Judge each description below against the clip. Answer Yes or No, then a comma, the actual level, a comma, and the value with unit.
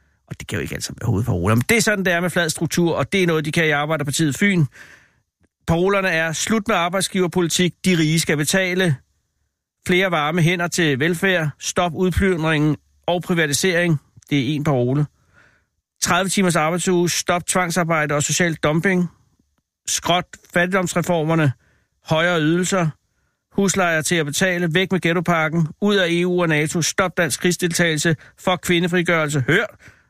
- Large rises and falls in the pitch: No, average, 2.9 semitones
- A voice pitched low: No, medium, 170 Hz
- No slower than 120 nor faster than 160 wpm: Yes, average, 150 wpm